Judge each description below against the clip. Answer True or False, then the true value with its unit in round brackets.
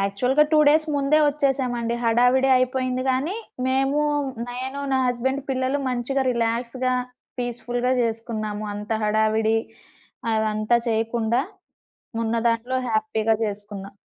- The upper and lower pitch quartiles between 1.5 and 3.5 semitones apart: True (2.9 semitones)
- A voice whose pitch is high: True (240 Hz)